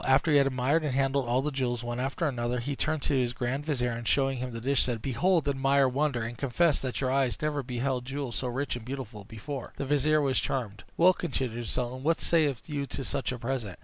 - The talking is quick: Yes, fast, 240 wpm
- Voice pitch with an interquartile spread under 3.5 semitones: Yes, narrow, 2.6 semitones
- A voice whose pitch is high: No, low, 135 Hz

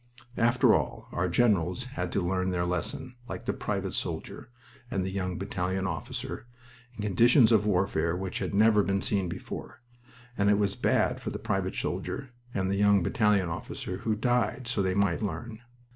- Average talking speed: Yes, average, 175 wpm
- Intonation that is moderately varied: Yes, average, 3.3 semitones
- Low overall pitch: Yes, low, 100 Hz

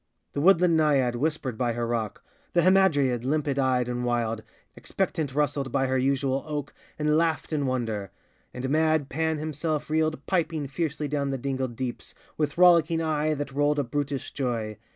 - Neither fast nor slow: Yes, average, 170 wpm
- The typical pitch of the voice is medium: Yes, medium, 145 Hz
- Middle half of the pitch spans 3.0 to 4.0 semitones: Yes, average, 3.4 semitones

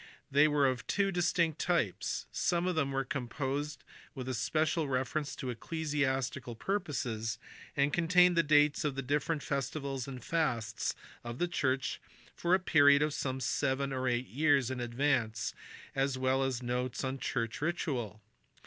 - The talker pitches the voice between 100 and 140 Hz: Yes, low, 135 Hz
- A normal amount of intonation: Yes, average, 3.3 semitones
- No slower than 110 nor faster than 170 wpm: Yes, average, 155 wpm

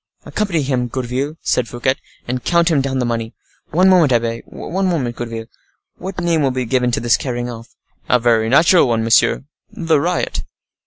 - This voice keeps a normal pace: Yes, average, 165 wpm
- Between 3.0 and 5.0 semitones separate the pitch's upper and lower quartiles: No, wide, 5.4 semitones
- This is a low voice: Yes, low, 130 Hz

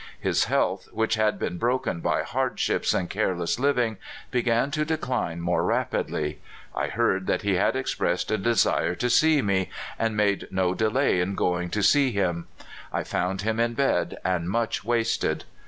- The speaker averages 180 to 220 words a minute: No, average, 170 wpm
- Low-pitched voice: Yes, low, 110 Hz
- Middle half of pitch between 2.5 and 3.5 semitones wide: No, average, 4.5 semitones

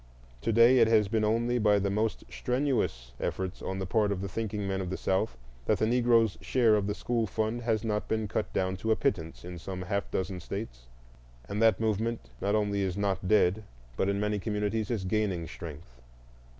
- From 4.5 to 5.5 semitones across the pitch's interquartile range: No, average, 2.8 semitones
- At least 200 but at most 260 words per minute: Yes, fast, 205 wpm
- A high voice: No, low, 105 Hz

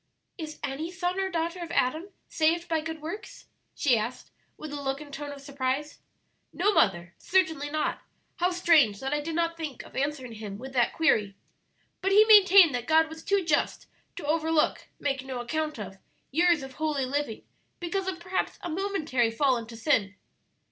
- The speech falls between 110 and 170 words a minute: No, average, 185 wpm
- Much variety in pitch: No, average, 4.4 semitones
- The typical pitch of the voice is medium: No, very high, 305 Hz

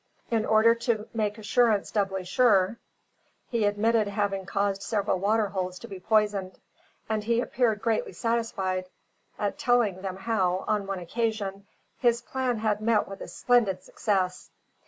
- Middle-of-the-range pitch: No, high, 210 Hz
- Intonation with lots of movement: No, average, 2.8 semitones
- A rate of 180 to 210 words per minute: No, average, 150 wpm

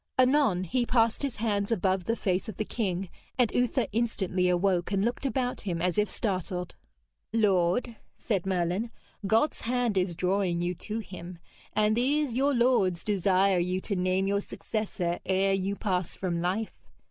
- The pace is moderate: Yes, average, 165 wpm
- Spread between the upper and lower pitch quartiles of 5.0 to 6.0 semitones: No, average, 4.0 semitones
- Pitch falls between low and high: No, high, 195 Hz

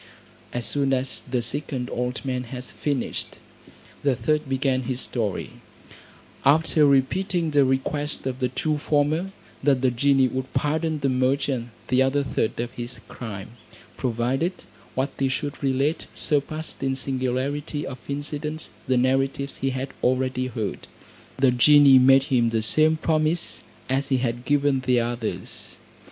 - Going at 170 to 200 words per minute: No, average, 145 wpm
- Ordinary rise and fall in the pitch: No, narrow, 2.3 semitones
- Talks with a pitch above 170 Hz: No, low, 135 Hz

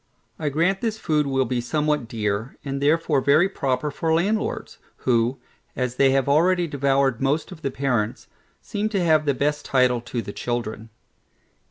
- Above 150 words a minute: Yes, average, 170 wpm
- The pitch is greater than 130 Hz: Yes, medium, 140 Hz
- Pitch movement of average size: Yes, average, 4.0 semitones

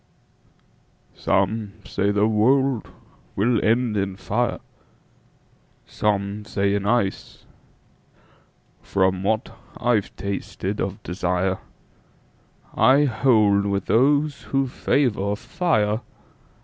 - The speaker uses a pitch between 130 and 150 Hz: No, low, 105 Hz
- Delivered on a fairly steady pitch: No, average, 3.6 semitones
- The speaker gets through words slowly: Yes, slow, 80 wpm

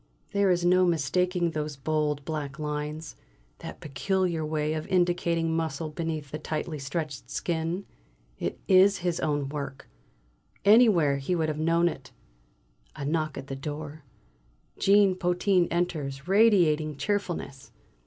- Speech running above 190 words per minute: No, slow, 135 wpm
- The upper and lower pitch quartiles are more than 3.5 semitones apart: No, average, 3.1 semitones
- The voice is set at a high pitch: No, medium, 160 Hz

